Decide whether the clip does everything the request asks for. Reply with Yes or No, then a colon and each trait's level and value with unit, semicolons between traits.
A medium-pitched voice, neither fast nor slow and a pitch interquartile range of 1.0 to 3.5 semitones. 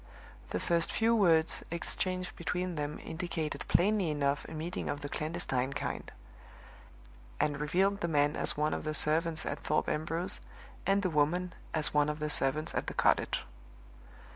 Yes: medium, 160 Hz; average, 165 wpm; average, 3.1 semitones